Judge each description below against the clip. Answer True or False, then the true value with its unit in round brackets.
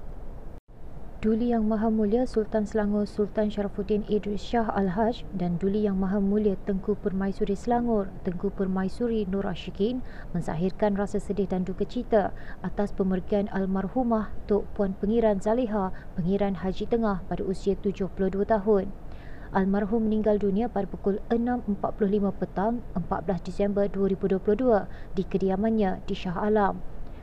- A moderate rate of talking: True (130 wpm)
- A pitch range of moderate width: False (2.0 semitones)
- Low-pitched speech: False (205 Hz)